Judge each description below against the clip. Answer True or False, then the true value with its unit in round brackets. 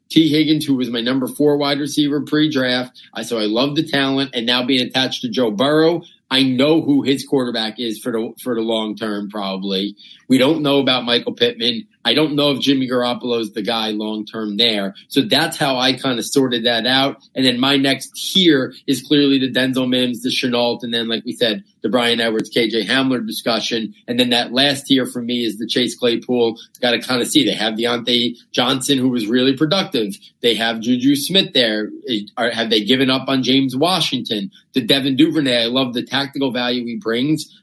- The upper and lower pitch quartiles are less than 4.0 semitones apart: True (3.2 semitones)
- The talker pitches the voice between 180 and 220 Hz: False (130 Hz)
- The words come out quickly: True (210 wpm)